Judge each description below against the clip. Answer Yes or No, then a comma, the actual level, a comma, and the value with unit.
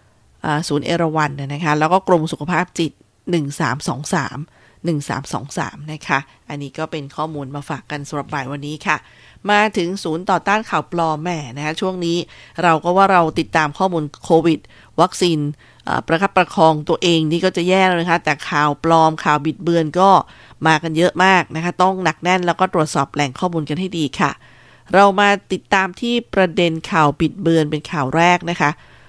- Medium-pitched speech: Yes, medium, 160 Hz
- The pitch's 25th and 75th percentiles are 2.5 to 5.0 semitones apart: Yes, average, 3.2 semitones